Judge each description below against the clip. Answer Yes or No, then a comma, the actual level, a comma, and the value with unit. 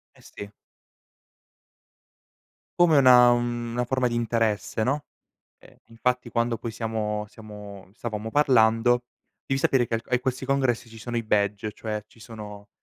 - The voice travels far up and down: No, narrow, 2.4 semitones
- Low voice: Yes, low, 115 Hz